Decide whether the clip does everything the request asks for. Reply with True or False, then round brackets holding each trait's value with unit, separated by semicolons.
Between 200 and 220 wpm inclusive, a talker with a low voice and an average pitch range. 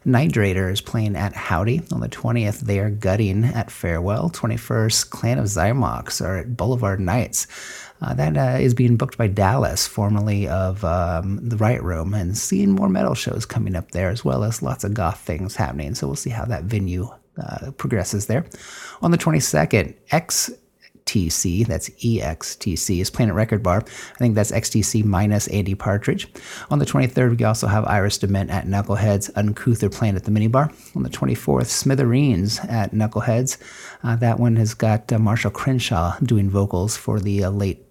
False (180 wpm; 110 Hz; 3.4 semitones)